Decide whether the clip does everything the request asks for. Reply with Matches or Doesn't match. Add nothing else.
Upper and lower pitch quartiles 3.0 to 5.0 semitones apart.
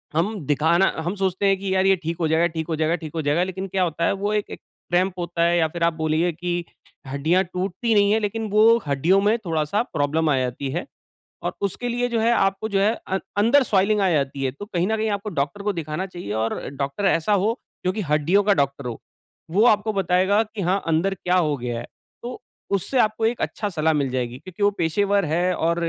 Matches